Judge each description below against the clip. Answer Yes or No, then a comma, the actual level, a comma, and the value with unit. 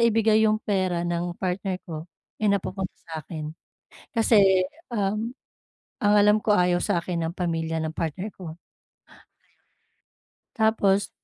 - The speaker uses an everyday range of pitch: Yes, average, 3.5 semitones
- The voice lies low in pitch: No, high, 190 Hz